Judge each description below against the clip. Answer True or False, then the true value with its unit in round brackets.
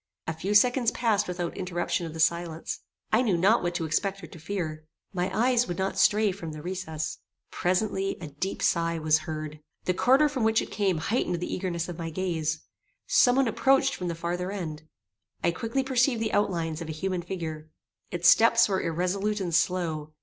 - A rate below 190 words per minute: False (195 wpm)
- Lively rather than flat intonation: False (4.0 semitones)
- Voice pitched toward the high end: False (180 Hz)